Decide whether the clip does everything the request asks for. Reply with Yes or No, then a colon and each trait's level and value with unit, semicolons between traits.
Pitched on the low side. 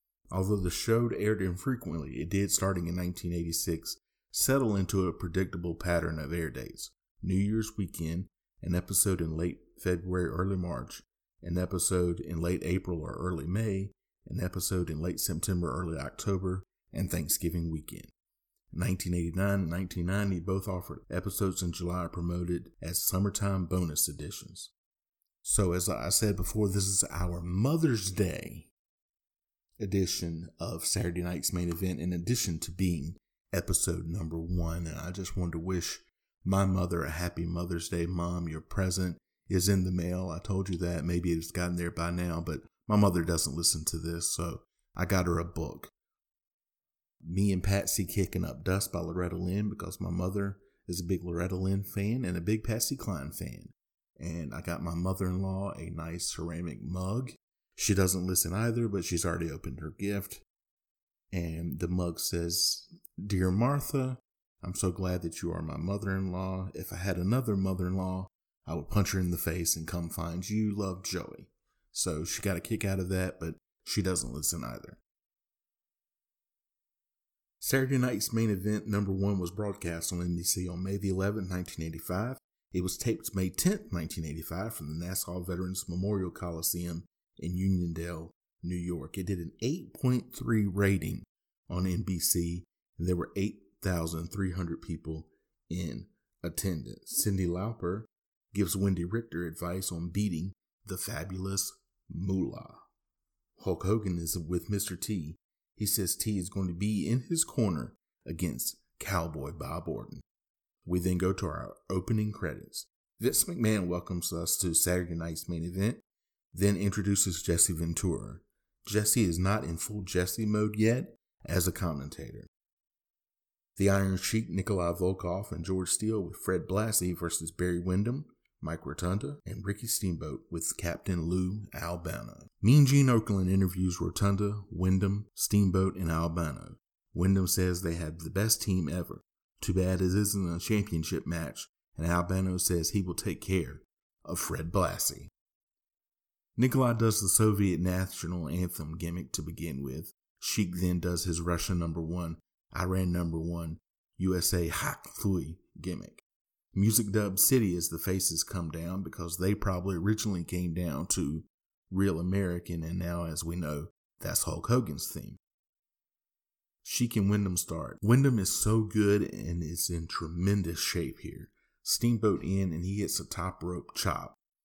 Yes: very low, 90 Hz